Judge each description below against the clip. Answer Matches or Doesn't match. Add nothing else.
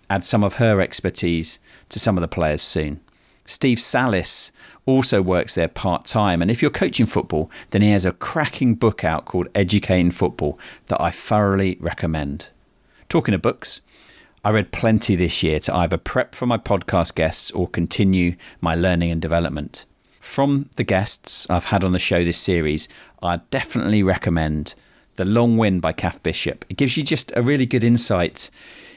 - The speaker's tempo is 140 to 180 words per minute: Matches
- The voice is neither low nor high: Doesn't match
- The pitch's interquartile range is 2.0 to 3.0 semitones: Doesn't match